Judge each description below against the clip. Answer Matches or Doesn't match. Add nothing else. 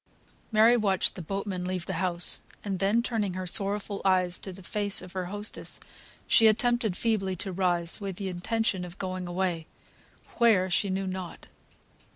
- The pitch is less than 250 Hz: Matches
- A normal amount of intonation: Doesn't match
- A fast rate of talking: Doesn't match